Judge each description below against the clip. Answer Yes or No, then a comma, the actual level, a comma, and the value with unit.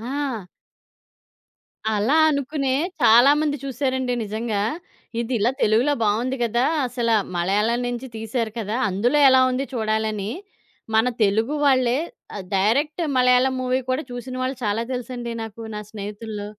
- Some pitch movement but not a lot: Yes, average, 3.2 semitones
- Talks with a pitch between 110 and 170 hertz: No, high, 240 Hz